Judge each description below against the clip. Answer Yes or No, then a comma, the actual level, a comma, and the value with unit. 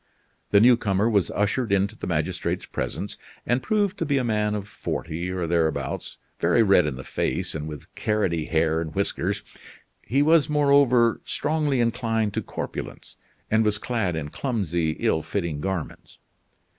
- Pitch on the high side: No, low, 105 Hz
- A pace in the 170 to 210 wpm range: No, average, 155 wpm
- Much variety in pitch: Yes, wide, 6.3 semitones